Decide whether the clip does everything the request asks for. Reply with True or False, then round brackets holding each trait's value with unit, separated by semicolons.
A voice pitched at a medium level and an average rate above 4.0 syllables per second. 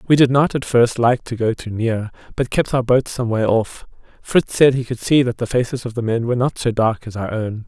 False (120 Hz; 5.4 syllables/s)